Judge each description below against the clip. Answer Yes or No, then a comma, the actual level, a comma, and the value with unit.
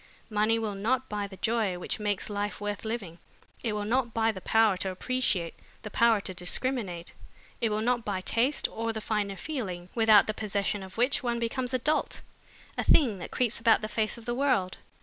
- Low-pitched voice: No, high, 220 Hz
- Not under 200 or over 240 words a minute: Yes, fast, 205 wpm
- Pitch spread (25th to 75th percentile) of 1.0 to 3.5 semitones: Yes, average, 2.9 semitones